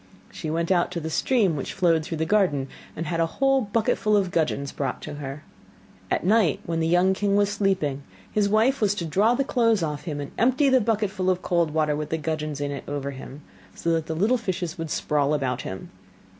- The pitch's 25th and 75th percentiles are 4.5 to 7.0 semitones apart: Yes, wide, 5.4 semitones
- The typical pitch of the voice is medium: Yes, medium, 170 Hz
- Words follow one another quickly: Yes, fast, 225 wpm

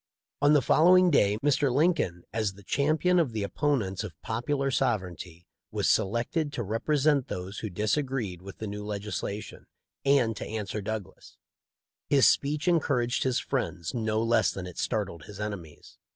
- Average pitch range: No, wide, 5.9 semitones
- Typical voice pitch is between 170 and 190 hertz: No, low, 110 Hz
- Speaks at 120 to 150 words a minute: No, average, 165 wpm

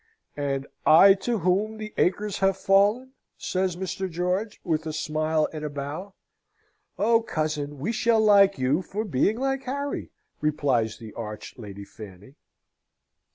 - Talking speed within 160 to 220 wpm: No, average, 145 wpm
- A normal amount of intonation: No, wide, 6.4 semitones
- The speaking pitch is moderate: Yes, medium, 180 Hz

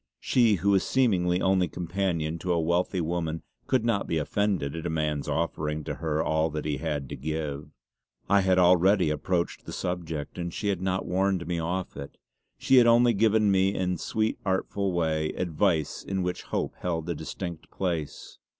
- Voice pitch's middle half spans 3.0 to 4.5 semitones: Yes, average, 3.4 semitones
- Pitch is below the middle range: Yes, very low, 90 Hz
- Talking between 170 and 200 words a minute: Yes, average, 185 wpm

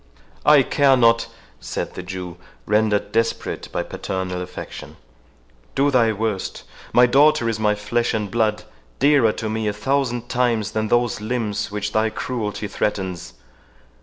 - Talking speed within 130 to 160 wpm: Yes, average, 145 wpm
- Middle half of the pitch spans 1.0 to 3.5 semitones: Yes, average, 2.8 semitones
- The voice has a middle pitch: No, low, 110 Hz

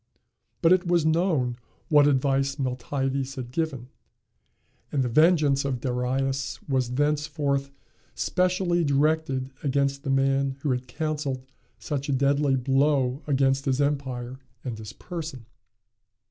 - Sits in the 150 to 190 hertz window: No, medium, 140 Hz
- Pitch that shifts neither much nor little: No, narrow, 2.3 semitones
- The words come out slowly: Yes, slow, 125 wpm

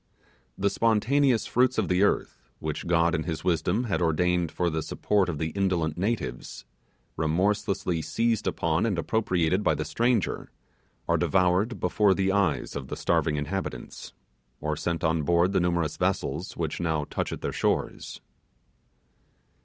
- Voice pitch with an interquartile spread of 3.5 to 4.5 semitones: Yes, average, 4.0 semitones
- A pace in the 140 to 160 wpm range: Yes, average, 155 wpm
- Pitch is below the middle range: Yes, very low, 90 Hz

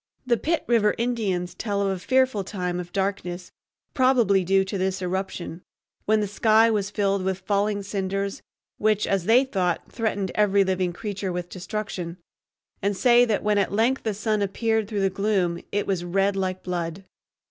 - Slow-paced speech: No, average, 175 wpm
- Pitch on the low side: No, high, 200 Hz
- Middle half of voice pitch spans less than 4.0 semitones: Yes, narrow, 2.5 semitones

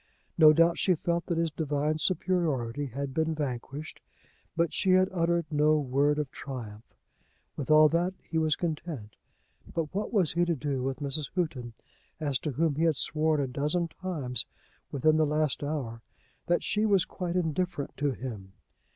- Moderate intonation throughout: Yes, average, 3.4 semitones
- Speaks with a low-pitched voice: No, medium, 155 Hz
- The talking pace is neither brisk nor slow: Yes, average, 170 wpm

